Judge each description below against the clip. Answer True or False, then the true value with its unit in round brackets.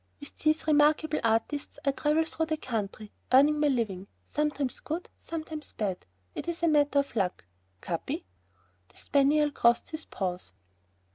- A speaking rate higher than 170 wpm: False (150 wpm)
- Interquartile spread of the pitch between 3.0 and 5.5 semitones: True (5.0 semitones)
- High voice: True (290 Hz)